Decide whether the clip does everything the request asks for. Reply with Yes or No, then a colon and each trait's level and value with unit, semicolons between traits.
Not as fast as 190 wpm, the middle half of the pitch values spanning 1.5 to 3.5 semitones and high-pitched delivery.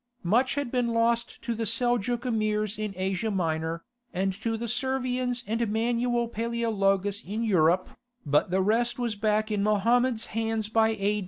Yes: average, 160 wpm; average, 2.8 semitones; high, 225 Hz